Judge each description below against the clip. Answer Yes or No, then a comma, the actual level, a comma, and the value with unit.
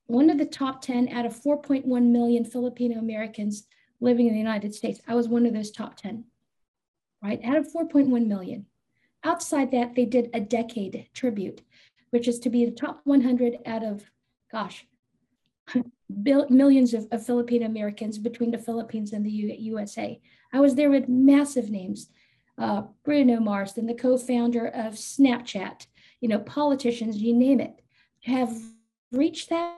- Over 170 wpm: No, average, 160 wpm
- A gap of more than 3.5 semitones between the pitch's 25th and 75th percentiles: No, average, 2.7 semitones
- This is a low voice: No, high, 240 Hz